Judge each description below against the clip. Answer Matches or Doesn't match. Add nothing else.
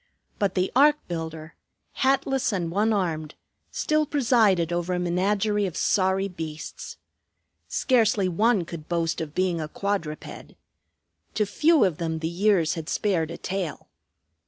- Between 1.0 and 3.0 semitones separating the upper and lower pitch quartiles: Doesn't match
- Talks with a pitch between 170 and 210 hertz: Matches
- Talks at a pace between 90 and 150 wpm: Matches